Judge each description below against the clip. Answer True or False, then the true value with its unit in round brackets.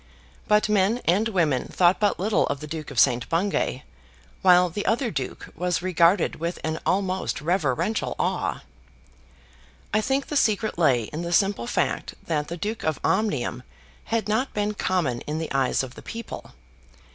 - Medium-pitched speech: True (180 Hz)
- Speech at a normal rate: True (170 wpm)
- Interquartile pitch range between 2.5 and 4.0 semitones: False (5.4 semitones)